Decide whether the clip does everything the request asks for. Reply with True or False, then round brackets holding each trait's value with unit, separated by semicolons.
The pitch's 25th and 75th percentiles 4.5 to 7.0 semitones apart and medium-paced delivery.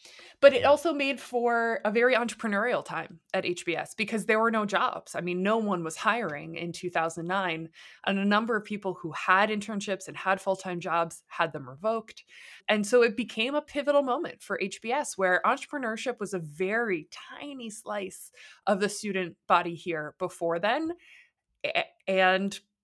True (4.9 semitones; 170 wpm)